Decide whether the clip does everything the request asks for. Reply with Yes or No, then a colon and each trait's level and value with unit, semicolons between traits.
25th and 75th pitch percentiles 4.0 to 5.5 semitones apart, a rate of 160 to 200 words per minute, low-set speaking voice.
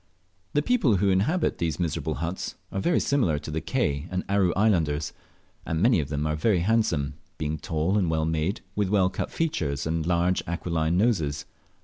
Yes: average, 4.3 semitones; average, 180 wpm; very low, 85 Hz